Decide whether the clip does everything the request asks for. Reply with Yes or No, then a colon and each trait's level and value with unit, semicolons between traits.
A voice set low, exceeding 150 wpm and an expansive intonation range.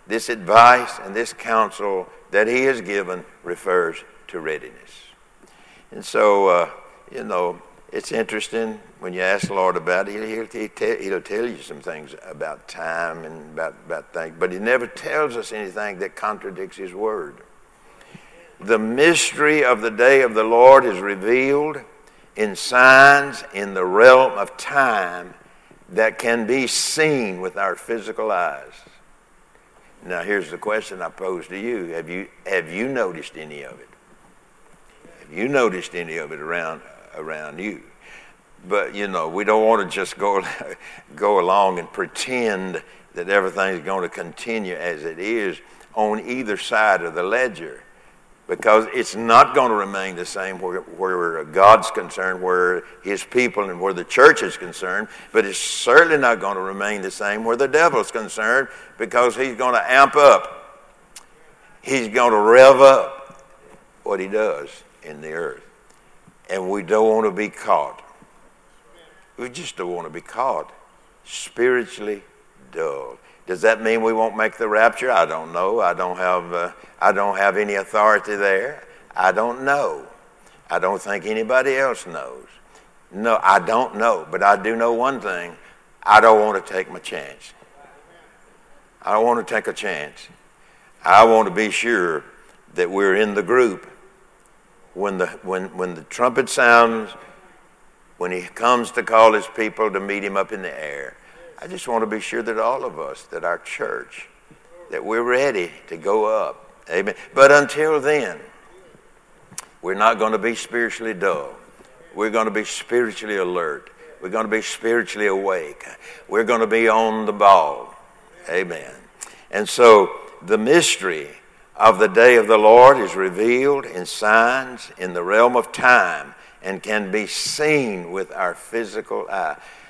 Yes: low, 115 Hz; average, 165 wpm; wide, 5.7 semitones